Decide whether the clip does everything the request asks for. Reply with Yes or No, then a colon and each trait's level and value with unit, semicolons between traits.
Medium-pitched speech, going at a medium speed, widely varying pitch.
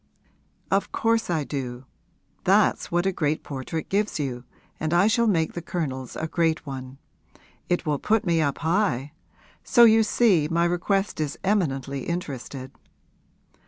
Yes: medium, 165 Hz; average, 150 wpm; wide, 5.7 semitones